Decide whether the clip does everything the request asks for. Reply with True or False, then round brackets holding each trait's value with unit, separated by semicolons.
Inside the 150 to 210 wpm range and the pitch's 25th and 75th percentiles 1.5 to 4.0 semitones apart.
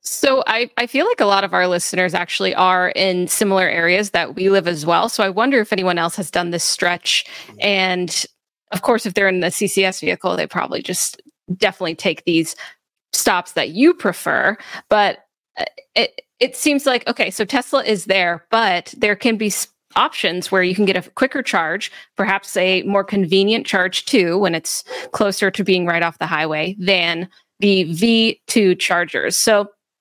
True (180 wpm; 3.4 semitones)